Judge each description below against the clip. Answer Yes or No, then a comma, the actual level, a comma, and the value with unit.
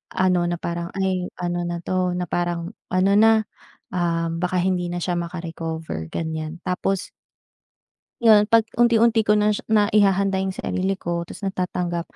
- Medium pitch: Yes, medium, 180 Hz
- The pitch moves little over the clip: Yes, narrow, 2.3 semitones